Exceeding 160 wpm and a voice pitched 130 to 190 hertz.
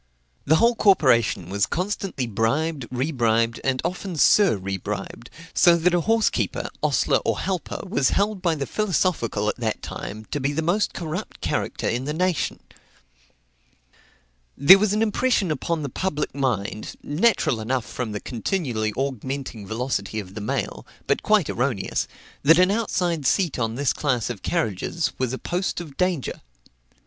No: average, 155 wpm; medium, 140 Hz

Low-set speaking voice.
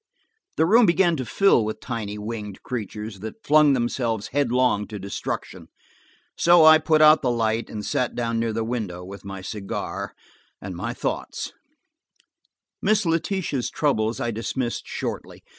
Yes: low, 115 Hz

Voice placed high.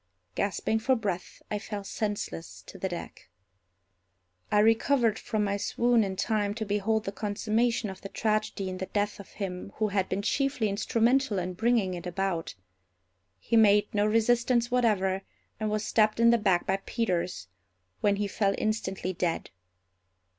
Yes: high, 210 Hz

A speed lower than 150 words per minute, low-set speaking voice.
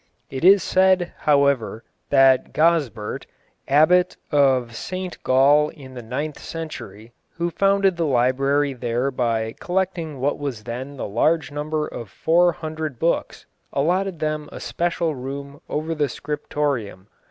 No: slow, 135 wpm; medium, 145 Hz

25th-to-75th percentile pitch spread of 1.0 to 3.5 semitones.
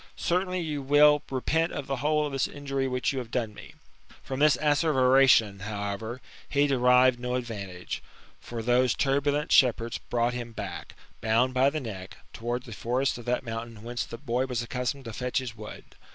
Yes: average, 3.0 semitones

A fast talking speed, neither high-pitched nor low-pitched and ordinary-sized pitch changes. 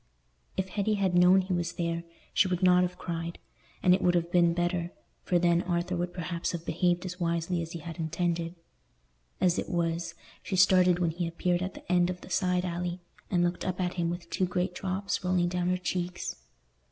No: fast, 210 wpm; medium, 175 Hz; narrow, 1.0 semitones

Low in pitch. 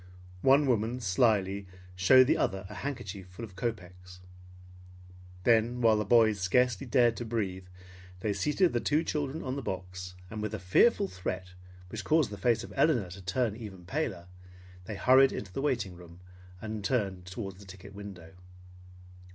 Yes: low, 105 Hz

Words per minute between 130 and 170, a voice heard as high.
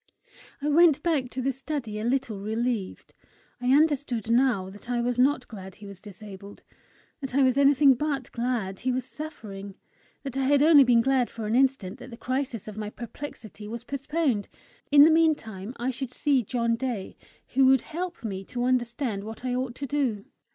No: average, 190 wpm; very high, 250 Hz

